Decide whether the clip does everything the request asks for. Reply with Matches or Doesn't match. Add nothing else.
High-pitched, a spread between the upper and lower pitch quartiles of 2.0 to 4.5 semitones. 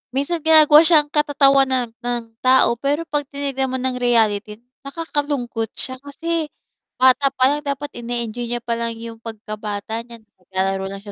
Matches